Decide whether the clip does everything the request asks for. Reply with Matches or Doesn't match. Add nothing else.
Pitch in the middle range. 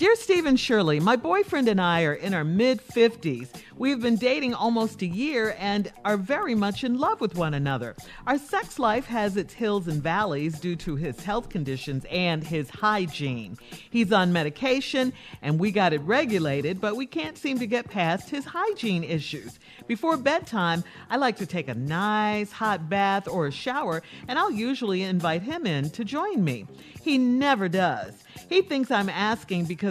Doesn't match